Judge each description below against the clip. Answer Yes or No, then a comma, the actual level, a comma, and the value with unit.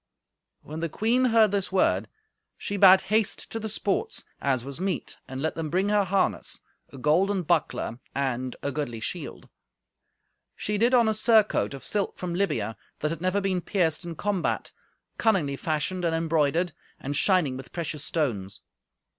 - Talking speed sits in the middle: Yes, average, 165 wpm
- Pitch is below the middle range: No, medium, 175 Hz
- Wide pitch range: Yes, wide, 5.8 semitones